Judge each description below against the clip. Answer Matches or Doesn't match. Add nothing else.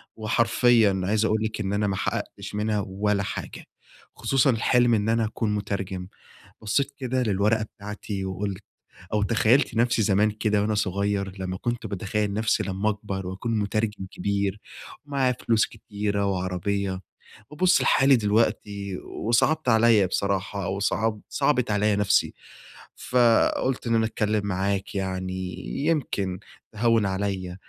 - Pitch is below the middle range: Matches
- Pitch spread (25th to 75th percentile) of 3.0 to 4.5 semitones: Doesn't match